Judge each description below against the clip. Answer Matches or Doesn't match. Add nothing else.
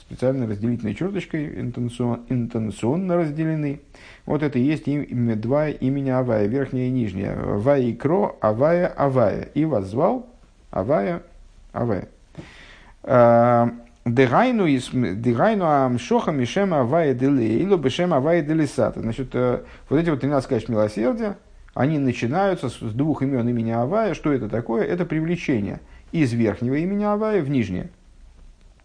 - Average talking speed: Matches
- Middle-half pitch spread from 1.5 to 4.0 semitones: Doesn't match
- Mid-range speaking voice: Doesn't match